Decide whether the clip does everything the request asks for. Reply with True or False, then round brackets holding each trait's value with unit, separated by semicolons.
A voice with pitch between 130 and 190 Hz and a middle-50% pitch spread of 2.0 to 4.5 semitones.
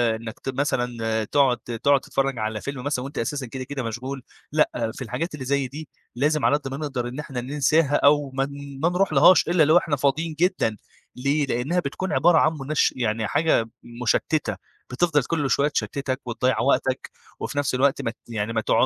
True (135 Hz; 3.3 semitones)